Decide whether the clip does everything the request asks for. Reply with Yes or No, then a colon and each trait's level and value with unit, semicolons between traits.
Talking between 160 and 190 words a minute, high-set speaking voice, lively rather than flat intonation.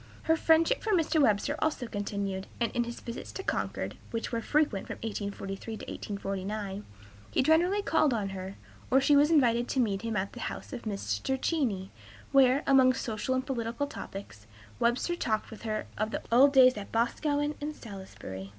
Yes: average, 180 wpm; high, 235 Hz; wide, 5.8 semitones